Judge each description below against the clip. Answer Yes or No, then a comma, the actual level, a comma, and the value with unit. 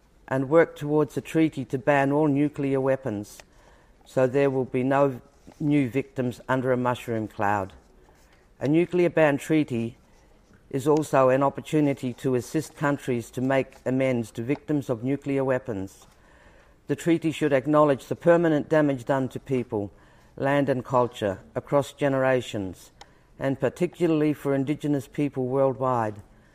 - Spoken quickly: No, average, 140 wpm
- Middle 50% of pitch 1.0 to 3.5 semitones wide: Yes, average, 2.8 semitones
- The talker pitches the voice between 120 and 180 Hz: Yes, low, 135 Hz